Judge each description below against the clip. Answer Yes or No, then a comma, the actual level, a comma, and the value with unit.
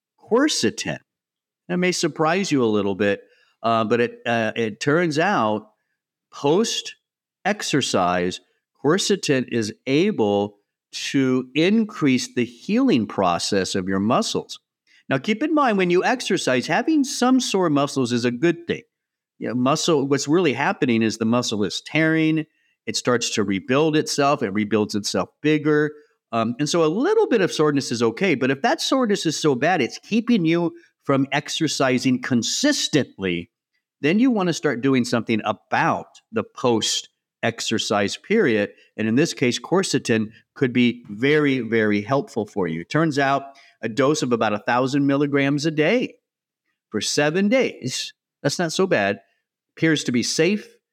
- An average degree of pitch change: No, wide, 6.6 semitones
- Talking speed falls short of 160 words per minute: Yes, average, 150 wpm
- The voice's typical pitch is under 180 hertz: Yes, medium, 140 Hz